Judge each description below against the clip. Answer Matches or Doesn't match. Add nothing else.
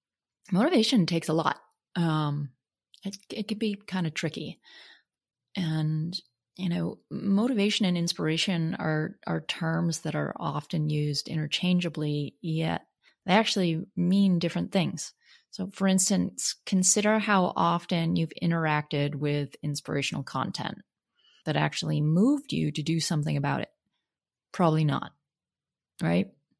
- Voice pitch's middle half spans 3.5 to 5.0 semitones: Matches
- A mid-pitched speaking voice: Matches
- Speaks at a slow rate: Matches